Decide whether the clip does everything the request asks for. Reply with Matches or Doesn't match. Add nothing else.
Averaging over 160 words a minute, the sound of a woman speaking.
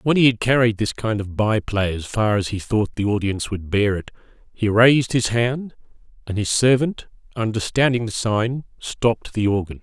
Doesn't match